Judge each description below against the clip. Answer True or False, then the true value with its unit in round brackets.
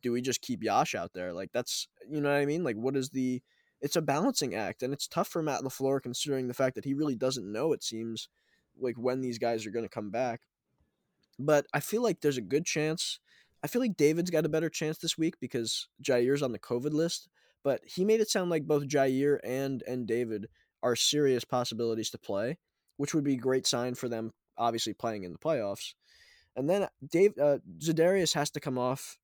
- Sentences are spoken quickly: True (225 wpm)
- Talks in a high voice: False (135 Hz)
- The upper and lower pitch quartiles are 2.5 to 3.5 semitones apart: False (4.0 semitones)